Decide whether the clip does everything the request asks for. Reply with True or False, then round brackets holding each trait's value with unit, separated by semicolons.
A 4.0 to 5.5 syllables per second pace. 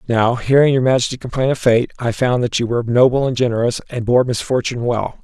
False (6.1 syllables/s)